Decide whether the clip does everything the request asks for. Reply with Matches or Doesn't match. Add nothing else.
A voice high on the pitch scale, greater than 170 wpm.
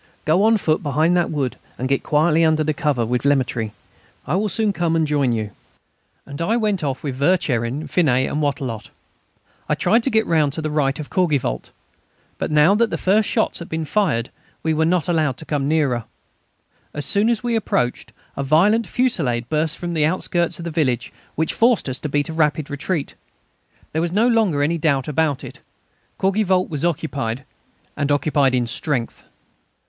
Doesn't match